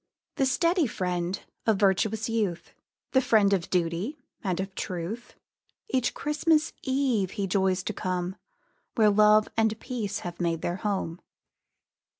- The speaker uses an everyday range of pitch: Yes, average, 3.9 semitones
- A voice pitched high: Yes, high, 205 Hz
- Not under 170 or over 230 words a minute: No, average, 140 wpm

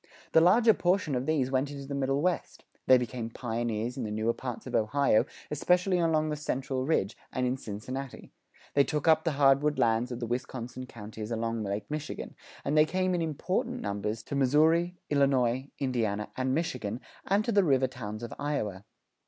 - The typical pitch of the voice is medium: No, low, 130 Hz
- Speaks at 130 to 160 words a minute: No, average, 185 wpm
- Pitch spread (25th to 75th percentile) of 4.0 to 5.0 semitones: Yes, average, 4.7 semitones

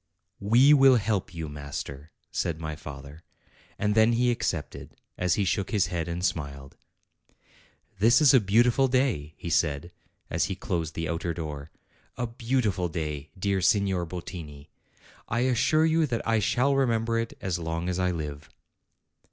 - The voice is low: Yes, very low, 90 Hz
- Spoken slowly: No, average, 160 wpm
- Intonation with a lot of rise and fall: Yes, wide, 6.3 semitones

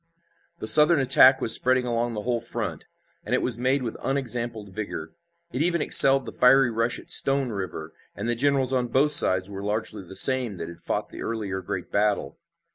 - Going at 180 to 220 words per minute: Yes, average, 200 wpm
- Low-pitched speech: Yes, low, 120 Hz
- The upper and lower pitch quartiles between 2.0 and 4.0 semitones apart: No, average, 4.4 semitones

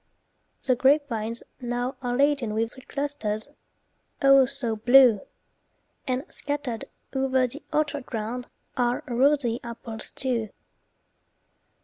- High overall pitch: Yes, very high, 250 Hz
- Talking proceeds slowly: Yes, slow, 105 wpm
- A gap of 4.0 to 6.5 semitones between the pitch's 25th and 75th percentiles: No, average, 2.8 semitones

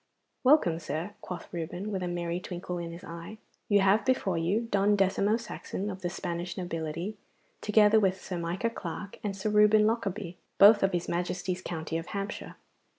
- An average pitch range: Yes, average, 3.2 semitones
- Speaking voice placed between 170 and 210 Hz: Yes, medium, 185 Hz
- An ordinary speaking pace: Yes, average, 175 wpm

